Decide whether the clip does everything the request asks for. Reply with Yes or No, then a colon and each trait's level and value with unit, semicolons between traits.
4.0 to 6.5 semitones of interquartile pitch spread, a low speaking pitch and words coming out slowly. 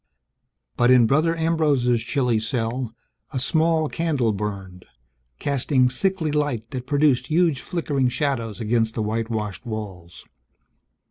Yes: average, 4.9 semitones; low, 125 Hz; slow, 120 wpm